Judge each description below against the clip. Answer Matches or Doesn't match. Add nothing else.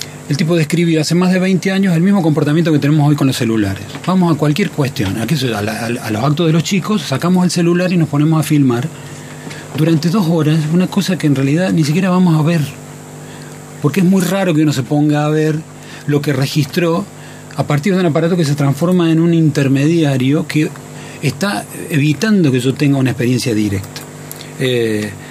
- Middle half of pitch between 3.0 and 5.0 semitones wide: Matches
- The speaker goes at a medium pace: Doesn't match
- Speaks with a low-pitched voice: Doesn't match